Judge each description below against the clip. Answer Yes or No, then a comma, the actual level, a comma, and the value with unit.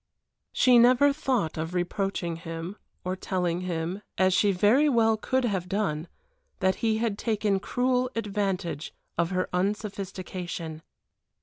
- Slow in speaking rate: Yes, slow, 130 wpm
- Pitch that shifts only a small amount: No, average, 4.0 semitones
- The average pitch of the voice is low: No, high, 195 Hz